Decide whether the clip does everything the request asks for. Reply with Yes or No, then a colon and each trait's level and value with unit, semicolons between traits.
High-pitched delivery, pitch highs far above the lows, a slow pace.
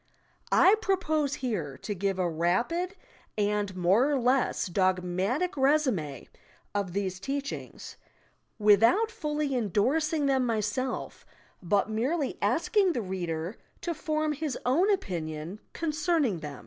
Yes: high, 240 Hz; wide, 8.4 semitones; slow, 120 wpm